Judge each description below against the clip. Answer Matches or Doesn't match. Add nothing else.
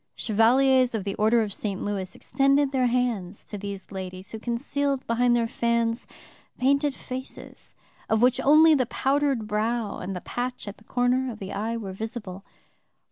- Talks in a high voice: Matches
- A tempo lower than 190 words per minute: Matches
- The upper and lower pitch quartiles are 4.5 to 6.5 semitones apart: Doesn't match